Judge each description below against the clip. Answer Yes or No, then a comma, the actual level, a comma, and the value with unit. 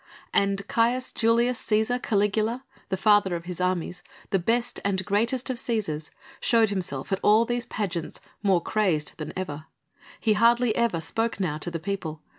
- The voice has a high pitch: Yes, high, 205 Hz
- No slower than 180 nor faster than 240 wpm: No, average, 165 wpm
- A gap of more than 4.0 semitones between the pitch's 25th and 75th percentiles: Yes, average, 4.6 semitones